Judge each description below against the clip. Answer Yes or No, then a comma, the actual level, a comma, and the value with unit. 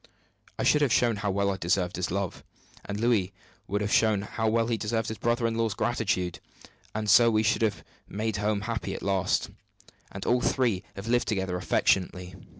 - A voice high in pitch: No, low, 105 Hz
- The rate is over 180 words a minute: Yes, average, 195 wpm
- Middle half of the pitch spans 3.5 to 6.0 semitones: No, average, 2.8 semitones